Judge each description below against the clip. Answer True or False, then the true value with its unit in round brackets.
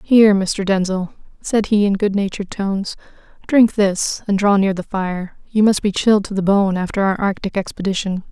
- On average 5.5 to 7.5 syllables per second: False (5.2 syllables/s)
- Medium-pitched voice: False (200 Hz)